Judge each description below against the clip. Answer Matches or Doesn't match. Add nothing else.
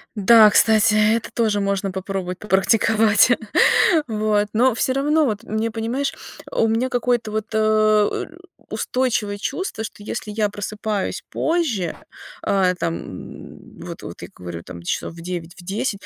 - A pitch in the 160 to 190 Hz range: Doesn't match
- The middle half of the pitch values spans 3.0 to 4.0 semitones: Doesn't match